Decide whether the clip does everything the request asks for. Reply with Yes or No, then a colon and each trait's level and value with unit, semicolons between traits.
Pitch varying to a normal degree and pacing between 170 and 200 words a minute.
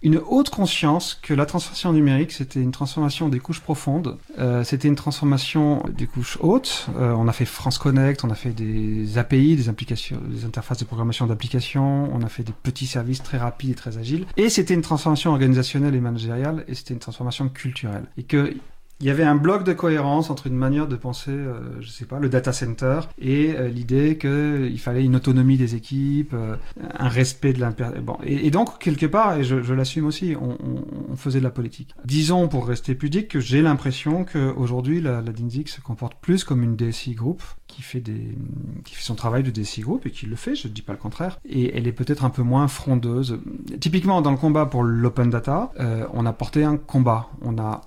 No: average, 3.5 semitones; fast, 220 wpm